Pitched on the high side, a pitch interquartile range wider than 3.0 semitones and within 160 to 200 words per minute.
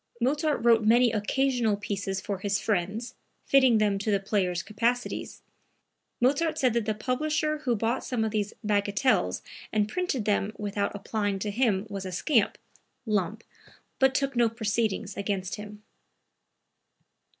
No: high, 215 Hz; average, 3.4 semitones; average, 145 wpm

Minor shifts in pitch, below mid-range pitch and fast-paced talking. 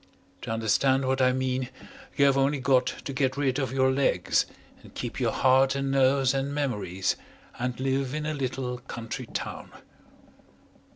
No: narrow, 1.3 semitones; low, 130 Hz; average, 165 wpm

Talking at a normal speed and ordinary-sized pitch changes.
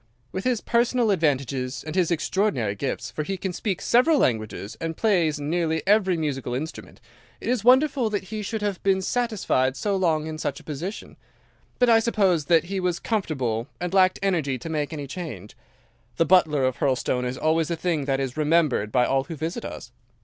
No: average, 185 wpm; wide, 6.0 semitones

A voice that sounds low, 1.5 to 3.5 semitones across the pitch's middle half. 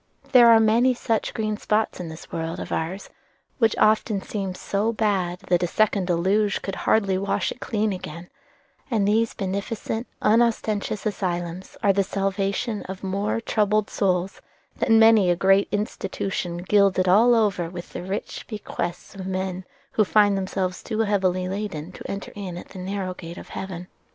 No: high, 195 Hz; narrow, 2.6 semitones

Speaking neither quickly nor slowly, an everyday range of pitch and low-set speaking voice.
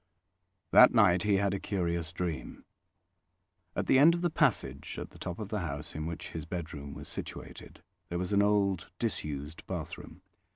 Yes: average, 175 wpm; average, 4.4 semitones; very low, 90 Hz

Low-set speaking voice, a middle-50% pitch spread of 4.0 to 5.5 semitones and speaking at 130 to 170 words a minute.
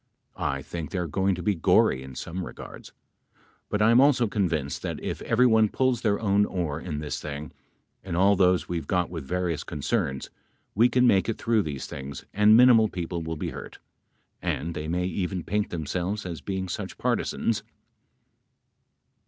No: very low, 90 Hz; average, 4.7 semitones; average, 180 wpm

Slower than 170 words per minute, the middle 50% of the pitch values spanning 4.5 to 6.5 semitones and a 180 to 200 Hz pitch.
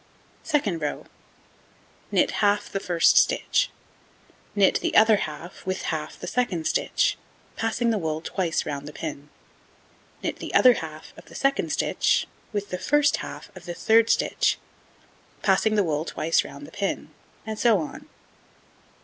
Yes: average, 155 wpm; wide, 5.5 semitones; high, 190 Hz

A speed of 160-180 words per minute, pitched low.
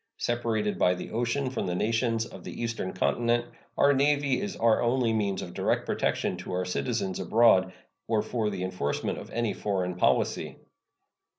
Yes: average, 170 wpm; low, 115 Hz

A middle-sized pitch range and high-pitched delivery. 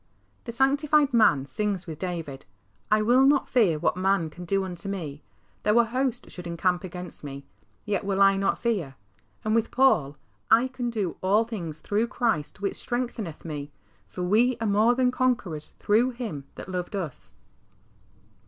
No: wide, 5.8 semitones; high, 200 Hz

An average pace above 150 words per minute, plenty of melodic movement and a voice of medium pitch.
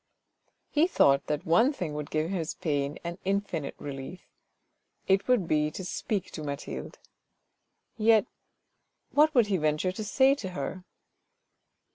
No: average, 140 wpm; wide, 5.7 semitones; medium, 180 Hz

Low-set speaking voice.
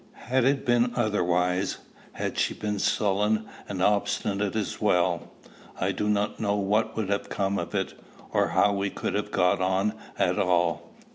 Yes: low, 100 Hz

